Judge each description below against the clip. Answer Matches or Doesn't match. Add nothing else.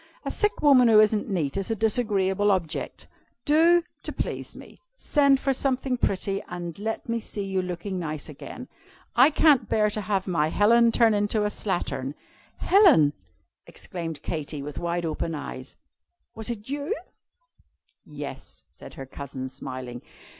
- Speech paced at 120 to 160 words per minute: Matches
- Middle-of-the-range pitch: Doesn't match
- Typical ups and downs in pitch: Doesn't match